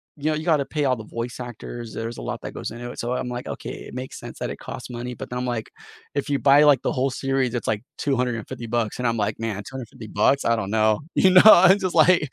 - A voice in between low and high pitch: No, low, 125 Hz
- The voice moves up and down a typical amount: Yes, average, 3.3 semitones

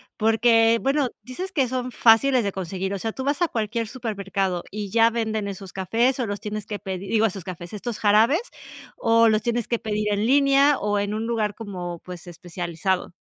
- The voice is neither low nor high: No, high, 215 Hz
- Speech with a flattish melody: No, average, 3.2 semitones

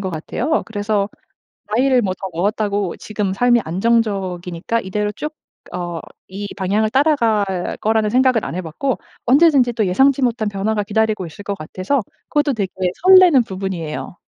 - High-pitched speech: Yes, high, 210 Hz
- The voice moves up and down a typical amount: Yes, average, 4.3 semitones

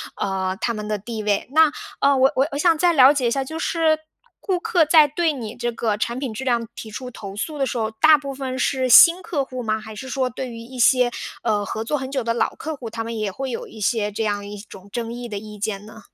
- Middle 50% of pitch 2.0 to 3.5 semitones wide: No, average, 4.1 semitones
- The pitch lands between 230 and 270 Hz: Yes, high, 240 Hz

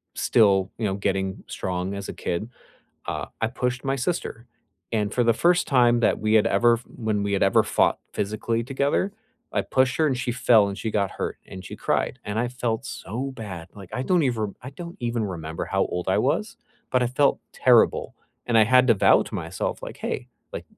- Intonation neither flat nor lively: Yes, average, 4.1 semitones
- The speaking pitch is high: No, low, 115 Hz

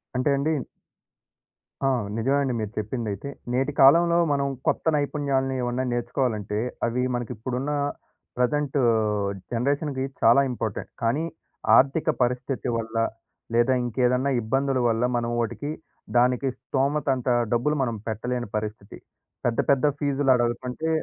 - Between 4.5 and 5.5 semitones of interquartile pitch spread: No, average, 2.9 semitones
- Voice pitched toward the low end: Yes, low, 125 Hz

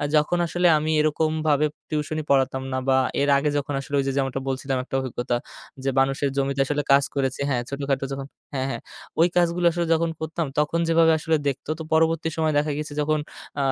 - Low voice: No, medium, 145 Hz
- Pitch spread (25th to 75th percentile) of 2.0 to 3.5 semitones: Yes, average, 2.7 semitones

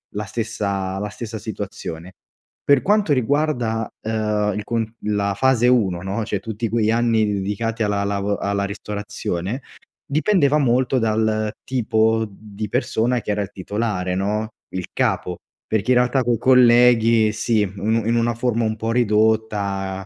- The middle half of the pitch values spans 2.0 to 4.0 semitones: Yes, narrow, 2.5 semitones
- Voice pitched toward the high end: No, low, 110 Hz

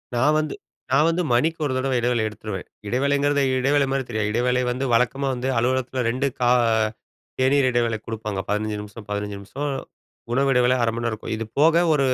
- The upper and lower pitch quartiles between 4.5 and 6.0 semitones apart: No, average, 3.5 semitones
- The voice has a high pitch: No, low, 125 Hz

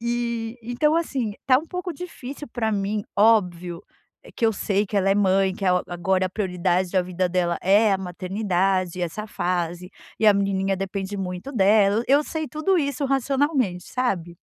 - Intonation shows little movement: No, average, 4.7 semitones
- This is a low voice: No, high, 200 Hz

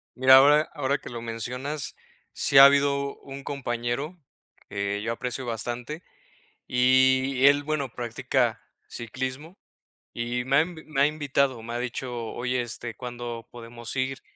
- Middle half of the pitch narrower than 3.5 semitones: Yes, average, 2.7 semitones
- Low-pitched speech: Yes, low, 130 Hz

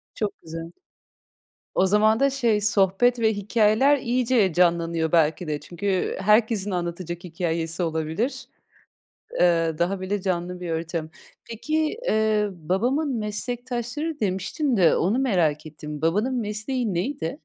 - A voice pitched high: Yes, high, 195 Hz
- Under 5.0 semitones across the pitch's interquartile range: No, wide, 5.6 semitones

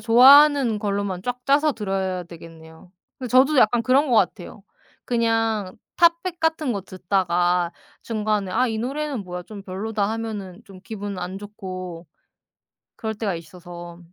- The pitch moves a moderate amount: Yes, average, 4.9 semitones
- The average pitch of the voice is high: Yes, high, 210 Hz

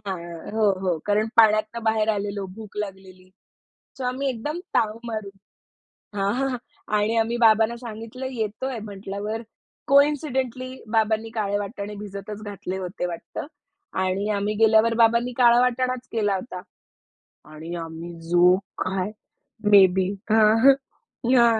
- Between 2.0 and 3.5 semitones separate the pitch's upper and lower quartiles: Yes, average, 3.1 semitones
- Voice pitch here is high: Yes, high, 215 Hz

